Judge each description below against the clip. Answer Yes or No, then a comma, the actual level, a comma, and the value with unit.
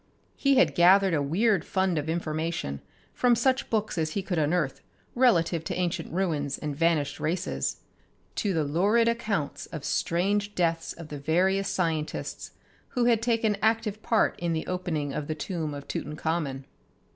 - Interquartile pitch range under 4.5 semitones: No, average, 4.8 semitones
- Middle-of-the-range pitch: Yes, medium, 170 Hz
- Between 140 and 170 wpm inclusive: Yes, average, 160 wpm